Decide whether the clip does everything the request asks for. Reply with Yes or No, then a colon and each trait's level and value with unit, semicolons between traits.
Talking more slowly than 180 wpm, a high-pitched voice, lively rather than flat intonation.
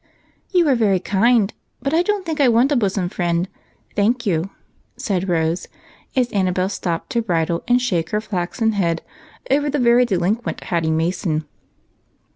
Yes: average, 155 wpm; high, 200 Hz; wide, 5.9 semitones